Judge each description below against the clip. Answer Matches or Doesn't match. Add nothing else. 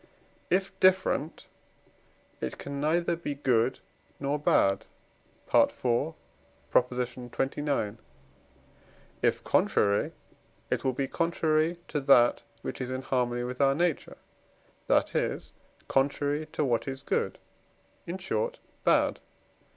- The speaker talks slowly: Matches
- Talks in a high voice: Doesn't match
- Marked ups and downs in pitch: Doesn't match